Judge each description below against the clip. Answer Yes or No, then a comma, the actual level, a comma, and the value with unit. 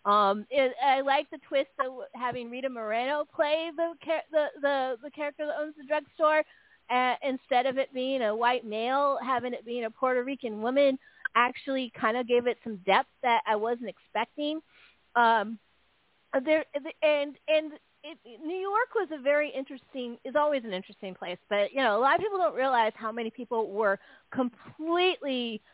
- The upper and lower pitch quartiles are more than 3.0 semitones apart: Yes, average, 4.1 semitones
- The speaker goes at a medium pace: Yes, average, 175 wpm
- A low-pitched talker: No, very high, 265 Hz